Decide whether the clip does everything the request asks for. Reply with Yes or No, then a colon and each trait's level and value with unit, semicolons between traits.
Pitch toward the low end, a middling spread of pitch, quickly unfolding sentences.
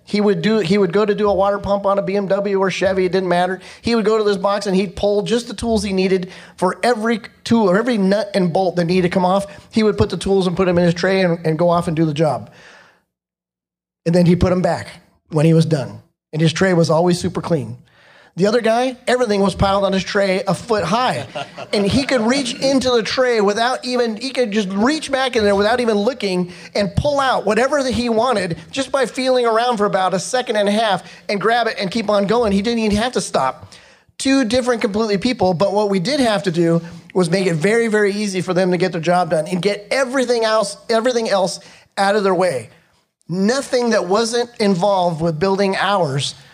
No: high, 200 Hz; average, 4.0 semitones; fast, 240 wpm